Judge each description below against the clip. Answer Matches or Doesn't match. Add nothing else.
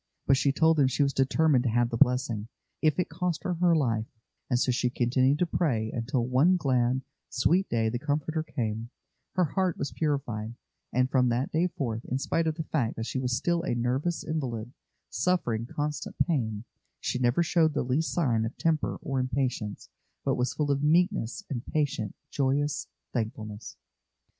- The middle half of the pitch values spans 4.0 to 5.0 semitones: Matches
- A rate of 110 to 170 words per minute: Doesn't match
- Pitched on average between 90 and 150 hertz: Matches